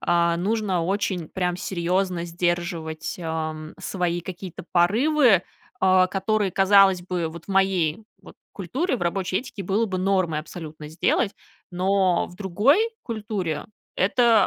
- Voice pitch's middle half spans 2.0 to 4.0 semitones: Yes, narrow, 2.6 semitones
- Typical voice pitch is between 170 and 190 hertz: Yes, medium, 185 Hz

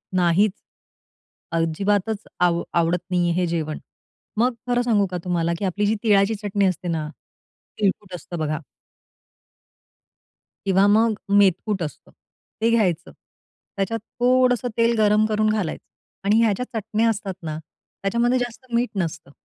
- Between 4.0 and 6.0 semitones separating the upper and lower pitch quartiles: Yes, average, 4.3 semitones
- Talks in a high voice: Yes, high, 200 Hz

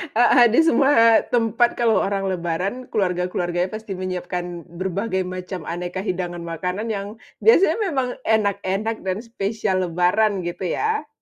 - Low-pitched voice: No, high, 190 Hz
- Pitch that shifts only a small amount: No, average, 3.6 semitones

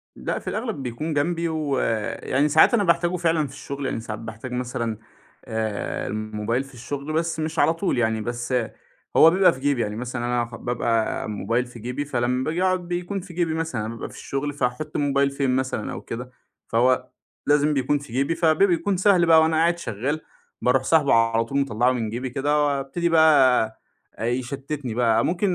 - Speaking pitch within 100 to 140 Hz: Yes, low, 135 Hz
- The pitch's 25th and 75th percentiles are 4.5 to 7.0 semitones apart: Yes, average, 4.9 semitones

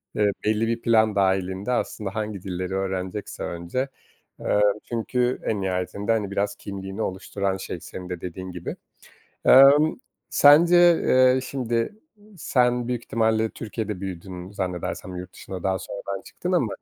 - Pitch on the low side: Yes, low, 100 Hz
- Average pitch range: Yes, average, 3.7 semitones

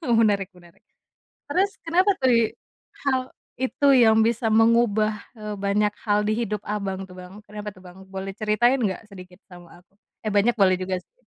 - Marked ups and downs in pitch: No, average, 3.3 semitones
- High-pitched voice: Yes, high, 210 Hz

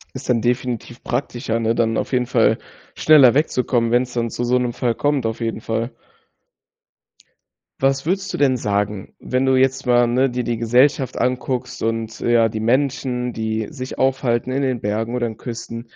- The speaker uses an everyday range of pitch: No, narrow, 2.2 semitones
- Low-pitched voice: Yes, low, 120 Hz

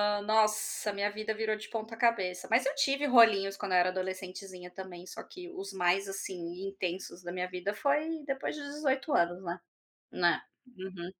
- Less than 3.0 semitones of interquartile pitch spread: No, average, 4.1 semitones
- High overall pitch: Yes, high, 200 Hz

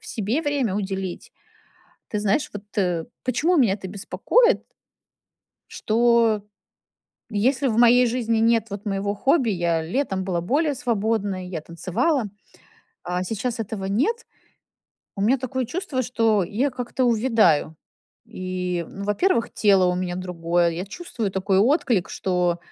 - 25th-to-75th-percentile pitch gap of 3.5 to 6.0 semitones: Yes, average, 5.0 semitones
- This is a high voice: Yes, high, 210 Hz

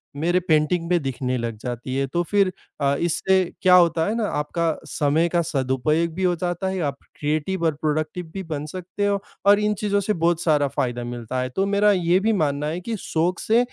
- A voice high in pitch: No, medium, 170 Hz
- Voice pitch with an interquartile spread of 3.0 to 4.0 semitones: No, average, 4.5 semitones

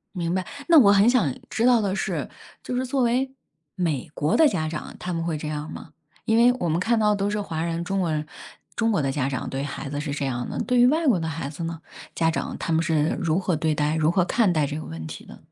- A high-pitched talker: No, medium, 170 Hz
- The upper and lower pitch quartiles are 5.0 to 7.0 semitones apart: Yes, wide, 5.6 semitones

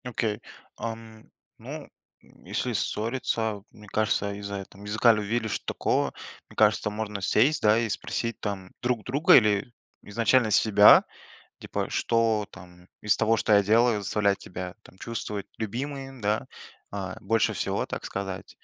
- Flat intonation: Yes, narrow, 2.3 semitones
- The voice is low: Yes, low, 105 Hz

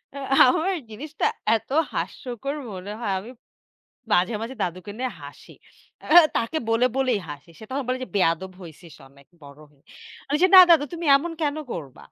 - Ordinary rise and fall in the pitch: No, wide, 7.9 semitones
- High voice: Yes, high, 225 Hz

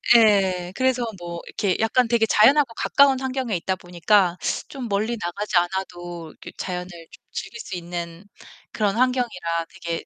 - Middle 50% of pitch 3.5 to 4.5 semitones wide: No, average, 5.2 semitones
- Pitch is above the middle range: Yes, high, 195 Hz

